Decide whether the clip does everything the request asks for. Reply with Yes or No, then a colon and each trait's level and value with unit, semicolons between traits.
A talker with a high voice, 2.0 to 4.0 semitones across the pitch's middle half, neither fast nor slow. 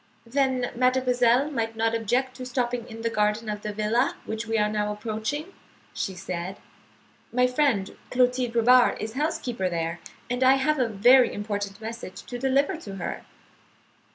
Yes: high, 235 Hz; average, 3.3 semitones; average, 160 wpm